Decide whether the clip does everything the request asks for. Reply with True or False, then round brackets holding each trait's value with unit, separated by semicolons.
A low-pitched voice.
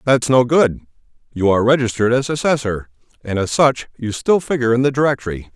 True (125 Hz)